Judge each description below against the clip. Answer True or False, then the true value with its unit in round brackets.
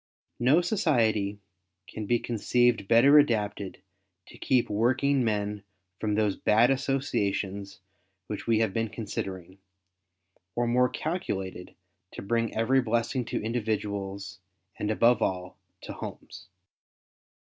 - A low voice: True (110 Hz)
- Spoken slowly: True (115 wpm)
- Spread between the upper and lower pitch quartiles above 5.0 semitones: False (3.4 semitones)